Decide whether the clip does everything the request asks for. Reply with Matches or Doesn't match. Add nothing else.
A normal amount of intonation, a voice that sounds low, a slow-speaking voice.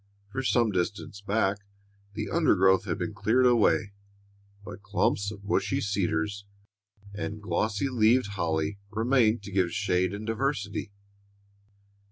Doesn't match